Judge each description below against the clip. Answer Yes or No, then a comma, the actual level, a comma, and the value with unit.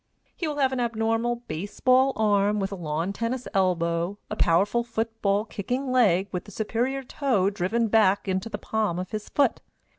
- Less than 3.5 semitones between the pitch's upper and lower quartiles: No, average, 3.8 semitones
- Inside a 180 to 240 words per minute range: Yes, average, 185 wpm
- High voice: Yes, high, 215 Hz